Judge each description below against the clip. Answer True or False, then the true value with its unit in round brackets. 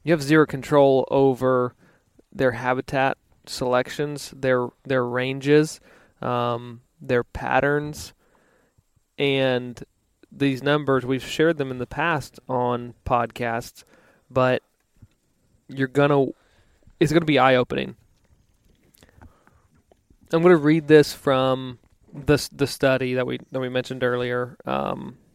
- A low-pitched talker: True (130 Hz)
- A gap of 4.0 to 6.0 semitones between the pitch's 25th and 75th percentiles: False (2.4 semitones)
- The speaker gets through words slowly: True (110 wpm)